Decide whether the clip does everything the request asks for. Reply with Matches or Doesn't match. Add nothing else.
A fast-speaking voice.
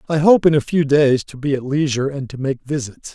Matches